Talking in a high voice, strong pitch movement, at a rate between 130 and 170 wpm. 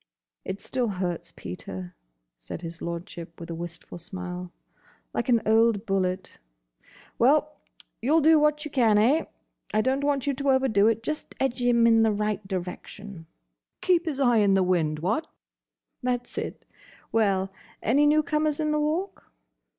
Yes: high, 220 Hz; wide, 7.5 semitones; average, 150 wpm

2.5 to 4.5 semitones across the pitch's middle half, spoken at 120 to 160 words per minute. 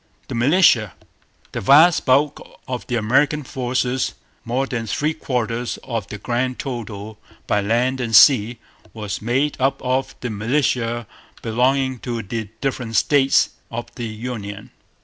Yes: average, 2.8 semitones; average, 140 wpm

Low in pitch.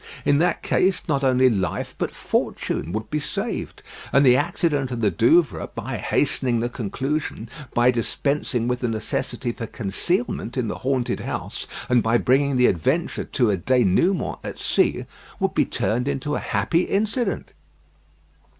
Yes: low, 125 Hz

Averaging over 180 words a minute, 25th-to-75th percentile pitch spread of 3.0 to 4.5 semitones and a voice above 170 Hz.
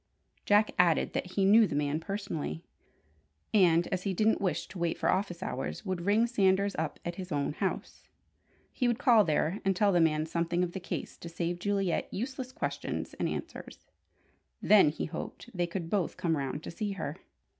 Yes: average, 190 wpm; average, 3.4 semitones; medium, 185 Hz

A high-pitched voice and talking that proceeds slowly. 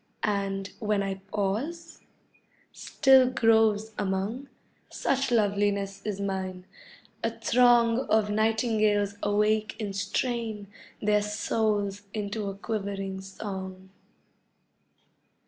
Yes: high, 210 Hz; slow, 95 wpm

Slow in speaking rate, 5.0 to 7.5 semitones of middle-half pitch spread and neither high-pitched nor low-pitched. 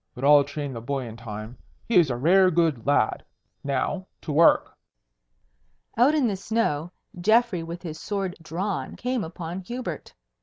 No: average, 160 wpm; wide, 5.6 semitones; medium, 165 Hz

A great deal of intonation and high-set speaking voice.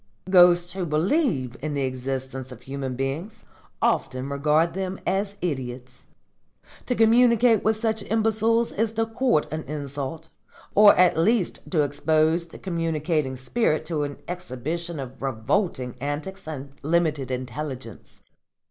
No: wide, 6.1 semitones; medium, 155 Hz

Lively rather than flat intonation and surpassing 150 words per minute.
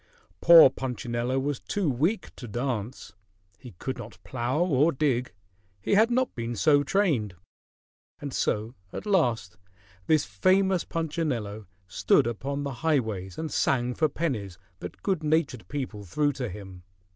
No: wide, 5.7 semitones; average, 145 wpm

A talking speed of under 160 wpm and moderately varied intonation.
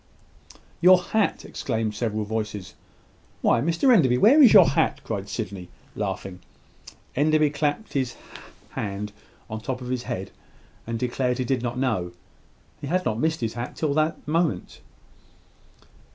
No: average, 150 wpm; wide, 6.2 semitones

